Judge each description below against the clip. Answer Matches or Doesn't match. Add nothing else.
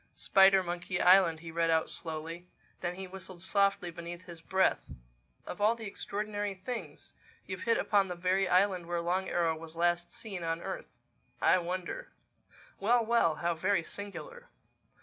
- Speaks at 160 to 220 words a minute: Doesn't match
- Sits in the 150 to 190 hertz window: Matches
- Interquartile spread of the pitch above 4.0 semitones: Doesn't match